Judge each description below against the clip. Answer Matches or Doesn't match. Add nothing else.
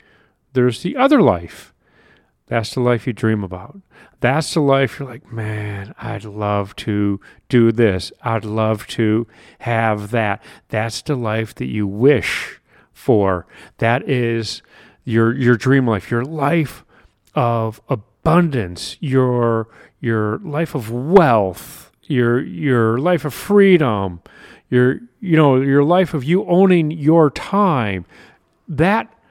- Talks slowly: Matches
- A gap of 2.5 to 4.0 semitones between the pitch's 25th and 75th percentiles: Doesn't match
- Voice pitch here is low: Matches